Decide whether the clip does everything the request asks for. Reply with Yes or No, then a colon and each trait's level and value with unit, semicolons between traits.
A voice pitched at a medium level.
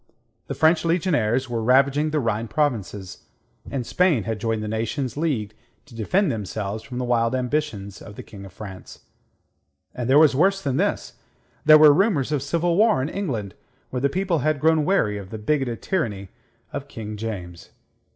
No: low, 130 Hz